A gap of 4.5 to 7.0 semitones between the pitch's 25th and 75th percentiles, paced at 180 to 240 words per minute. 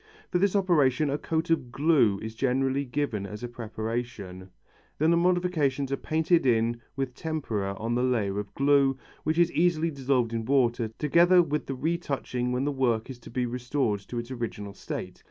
Yes: average, 4.8 semitones; average, 185 wpm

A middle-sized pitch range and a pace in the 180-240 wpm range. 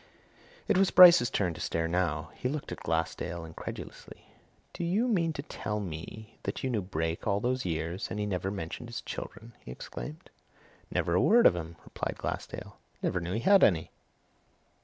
No: wide, 7.6 semitones; average, 185 wpm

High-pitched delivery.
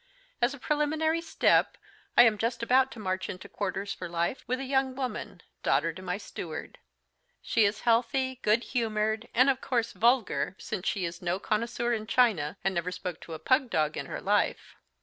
Yes: high, 225 Hz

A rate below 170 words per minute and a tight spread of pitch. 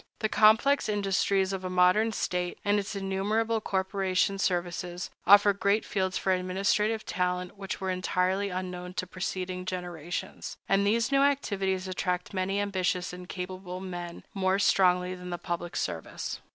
Yes: average, 150 wpm; narrow, 1.7 semitones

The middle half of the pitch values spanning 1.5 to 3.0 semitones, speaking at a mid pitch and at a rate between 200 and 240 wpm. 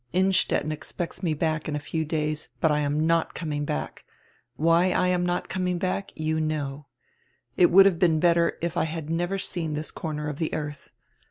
Yes: narrow, 2.6 semitones; medium, 160 Hz; fast, 205 wpm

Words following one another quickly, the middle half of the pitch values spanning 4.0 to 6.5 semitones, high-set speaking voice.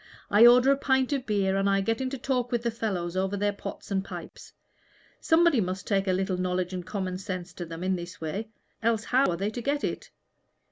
Yes: fast, 225 wpm; average, 4.6 semitones; high, 200 Hz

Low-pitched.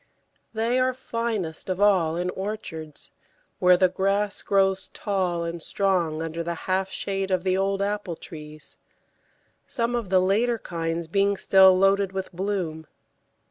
No: high, 190 Hz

